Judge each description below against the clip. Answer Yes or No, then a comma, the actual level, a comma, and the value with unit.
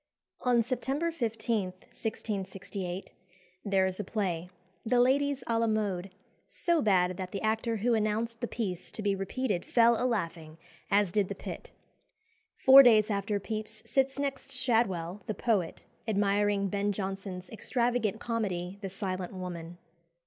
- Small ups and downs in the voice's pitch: No, average, 3.6 semitones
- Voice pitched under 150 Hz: No, high, 210 Hz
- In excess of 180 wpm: No, average, 145 wpm